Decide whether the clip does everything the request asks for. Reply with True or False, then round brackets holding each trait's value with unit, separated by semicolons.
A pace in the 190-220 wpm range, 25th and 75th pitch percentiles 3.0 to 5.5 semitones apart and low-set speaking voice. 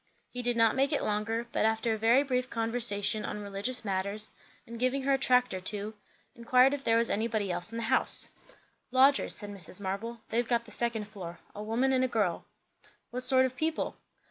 False (205 wpm; 3.3 semitones; 230 Hz)